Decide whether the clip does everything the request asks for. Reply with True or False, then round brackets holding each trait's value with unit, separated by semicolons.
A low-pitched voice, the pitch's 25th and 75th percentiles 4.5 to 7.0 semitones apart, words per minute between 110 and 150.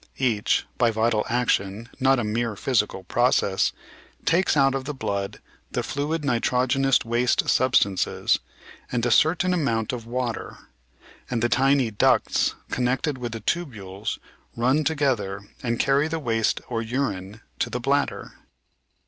False (120 Hz; 3.4 semitones; 145 wpm)